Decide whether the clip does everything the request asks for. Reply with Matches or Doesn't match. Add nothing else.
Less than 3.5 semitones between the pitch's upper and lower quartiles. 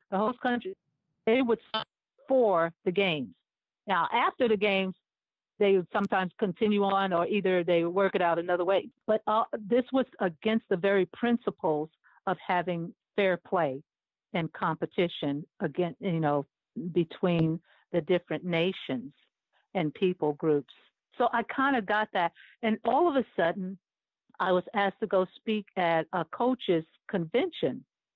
Doesn't match